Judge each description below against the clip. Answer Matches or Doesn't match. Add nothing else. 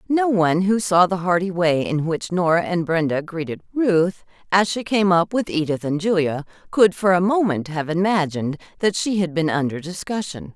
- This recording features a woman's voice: Matches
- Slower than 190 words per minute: Doesn't match